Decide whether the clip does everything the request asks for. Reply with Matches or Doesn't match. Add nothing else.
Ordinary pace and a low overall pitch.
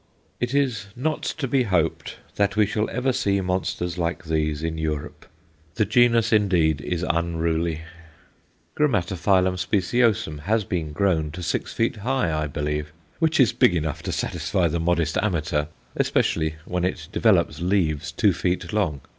Matches